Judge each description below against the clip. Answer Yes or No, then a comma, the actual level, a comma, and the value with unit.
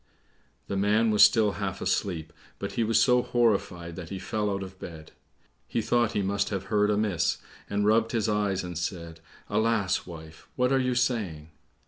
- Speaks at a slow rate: No, average, 180 wpm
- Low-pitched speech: Yes, low, 100 Hz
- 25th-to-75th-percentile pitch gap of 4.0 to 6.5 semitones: No, average, 3.3 semitones